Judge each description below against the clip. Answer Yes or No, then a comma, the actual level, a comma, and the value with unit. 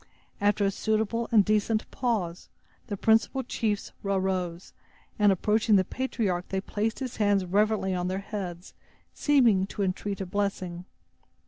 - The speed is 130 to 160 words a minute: Yes, average, 140 wpm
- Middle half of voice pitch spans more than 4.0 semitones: No, narrow, 2.6 semitones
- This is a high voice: Yes, high, 205 Hz